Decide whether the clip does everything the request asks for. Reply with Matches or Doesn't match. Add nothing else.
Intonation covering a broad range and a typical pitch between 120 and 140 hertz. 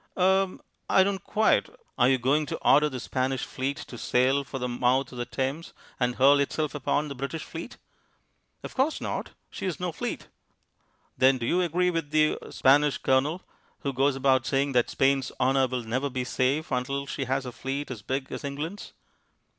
Doesn't match